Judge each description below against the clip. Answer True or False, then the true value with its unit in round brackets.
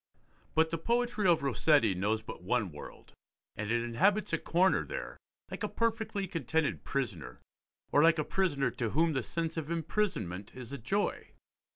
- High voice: False (160 Hz)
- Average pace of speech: True (170 wpm)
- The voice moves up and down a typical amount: False (8.0 semitones)